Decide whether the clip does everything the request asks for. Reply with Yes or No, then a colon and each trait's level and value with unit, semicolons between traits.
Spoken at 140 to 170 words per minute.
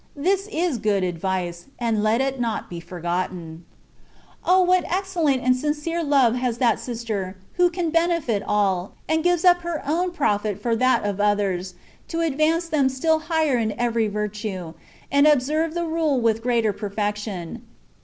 Yes: average, 160 wpm